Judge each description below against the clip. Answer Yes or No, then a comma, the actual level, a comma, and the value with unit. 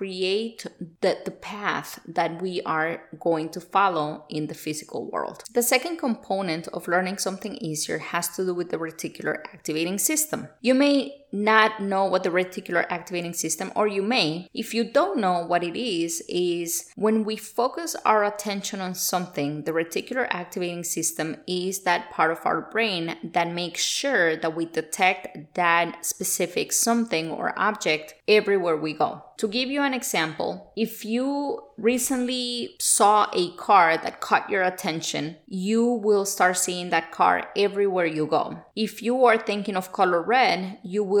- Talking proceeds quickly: No, average, 165 wpm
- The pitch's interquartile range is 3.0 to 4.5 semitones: Yes, average, 4.2 semitones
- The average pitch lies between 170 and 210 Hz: Yes, medium, 185 Hz